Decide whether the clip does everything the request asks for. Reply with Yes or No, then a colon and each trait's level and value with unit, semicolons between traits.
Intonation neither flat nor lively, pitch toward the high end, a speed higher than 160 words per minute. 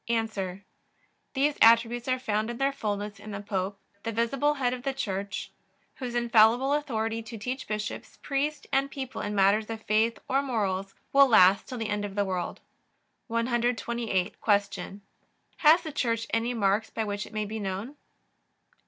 Yes: average, 3.5 semitones; high, 225 Hz; average, 170 wpm